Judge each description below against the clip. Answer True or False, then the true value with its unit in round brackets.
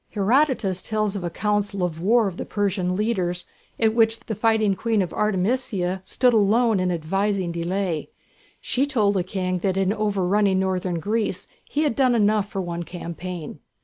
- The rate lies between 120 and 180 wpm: True (165 wpm)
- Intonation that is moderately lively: True (3.1 semitones)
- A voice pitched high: True (200 Hz)